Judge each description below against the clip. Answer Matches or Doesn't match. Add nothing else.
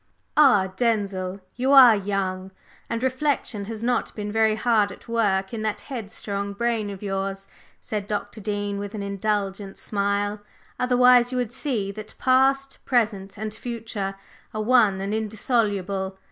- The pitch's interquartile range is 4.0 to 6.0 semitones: Doesn't match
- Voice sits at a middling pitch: Doesn't match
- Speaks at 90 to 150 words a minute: Matches